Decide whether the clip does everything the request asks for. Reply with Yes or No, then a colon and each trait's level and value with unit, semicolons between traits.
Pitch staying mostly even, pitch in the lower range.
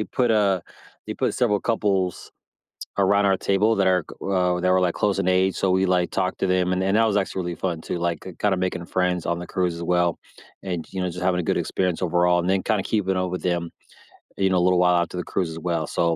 Yes: narrow, 1.5 semitones; very low, 90 Hz